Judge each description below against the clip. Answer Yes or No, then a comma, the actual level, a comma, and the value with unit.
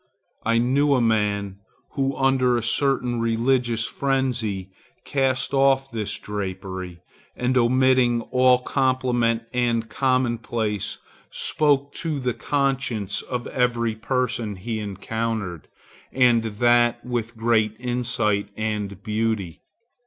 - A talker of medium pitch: No, low, 120 Hz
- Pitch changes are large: No, average, 3.0 semitones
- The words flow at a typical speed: No, slow, 110 wpm